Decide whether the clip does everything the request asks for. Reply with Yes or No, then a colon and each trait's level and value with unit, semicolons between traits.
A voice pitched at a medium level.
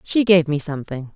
Yes: medium, 160 Hz